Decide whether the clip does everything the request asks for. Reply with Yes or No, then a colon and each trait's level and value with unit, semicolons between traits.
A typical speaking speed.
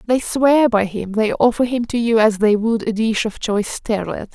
No: fast, 235 wpm